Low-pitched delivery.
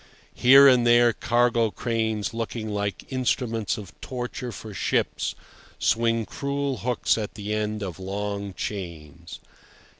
Yes: low, 110 Hz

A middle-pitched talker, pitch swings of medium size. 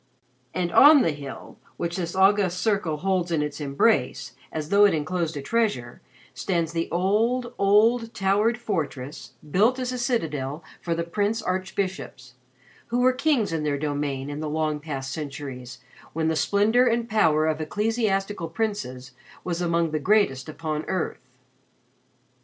No: medium, 170 Hz; wide, 5.7 semitones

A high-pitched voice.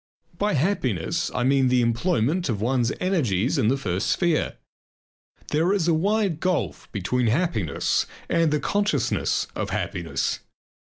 No: medium, 140 Hz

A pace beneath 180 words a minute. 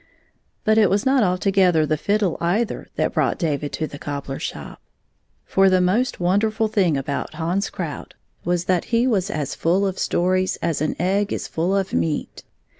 No: average, 185 wpm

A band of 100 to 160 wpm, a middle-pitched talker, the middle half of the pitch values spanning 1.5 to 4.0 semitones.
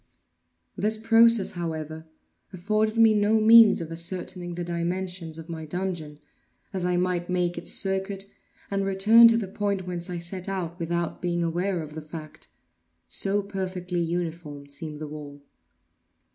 Yes: average, 150 wpm; medium, 180 Hz; average, 2.9 semitones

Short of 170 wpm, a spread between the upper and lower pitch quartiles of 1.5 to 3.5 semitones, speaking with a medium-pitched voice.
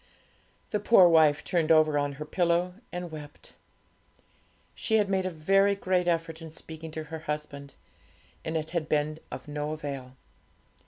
Yes: average, 160 wpm; average, 2.8 semitones; medium, 160 Hz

